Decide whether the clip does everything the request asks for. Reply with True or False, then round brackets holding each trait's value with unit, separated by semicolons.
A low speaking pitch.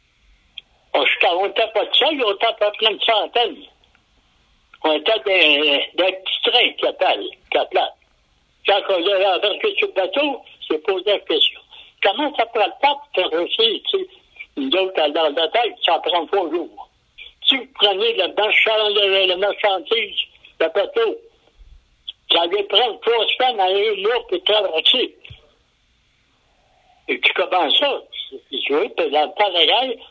False (240 Hz)